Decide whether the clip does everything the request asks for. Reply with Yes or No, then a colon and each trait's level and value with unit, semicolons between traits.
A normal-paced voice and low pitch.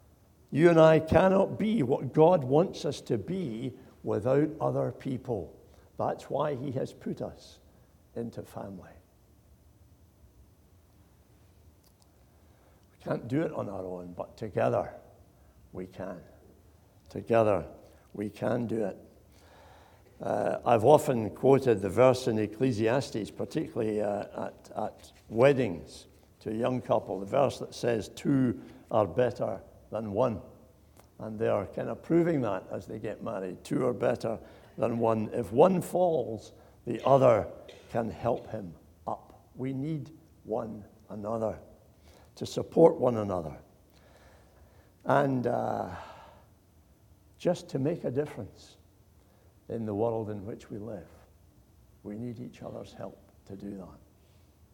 No: slow, 130 wpm; low, 105 Hz